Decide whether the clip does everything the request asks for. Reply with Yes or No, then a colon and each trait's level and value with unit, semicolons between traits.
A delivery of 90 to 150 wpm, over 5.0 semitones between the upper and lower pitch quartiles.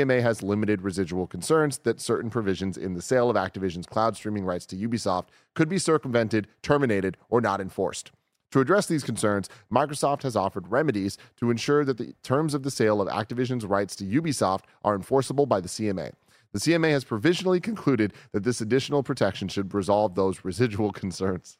No: average, 185 wpm; wide, 5.5 semitones